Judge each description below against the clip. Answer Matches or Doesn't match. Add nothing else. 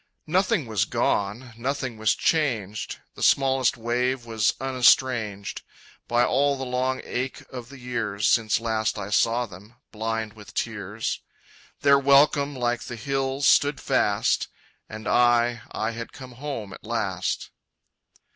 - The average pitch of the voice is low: Matches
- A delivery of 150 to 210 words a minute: Doesn't match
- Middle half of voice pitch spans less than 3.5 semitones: Matches